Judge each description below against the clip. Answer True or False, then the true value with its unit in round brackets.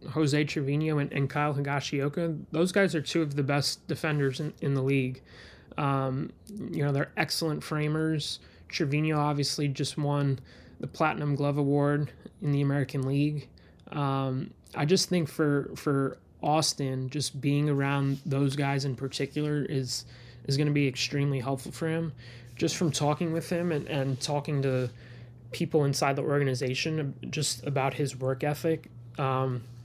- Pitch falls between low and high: True (145 Hz)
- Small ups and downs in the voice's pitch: True (2.0 semitones)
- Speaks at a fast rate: False (155 wpm)